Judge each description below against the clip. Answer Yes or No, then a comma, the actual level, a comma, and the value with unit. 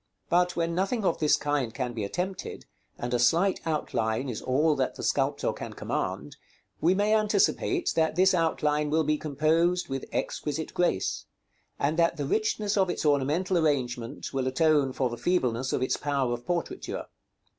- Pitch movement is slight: No, average, 5.3 semitones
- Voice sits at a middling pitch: Yes, medium, 155 Hz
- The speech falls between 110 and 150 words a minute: No, average, 170 wpm